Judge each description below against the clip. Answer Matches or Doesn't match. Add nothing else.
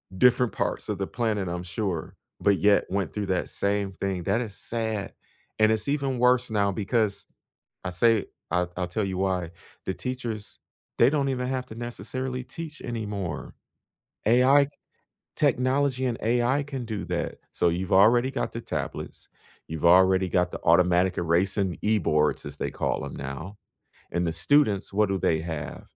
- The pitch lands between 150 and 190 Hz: Doesn't match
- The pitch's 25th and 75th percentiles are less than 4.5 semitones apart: Doesn't match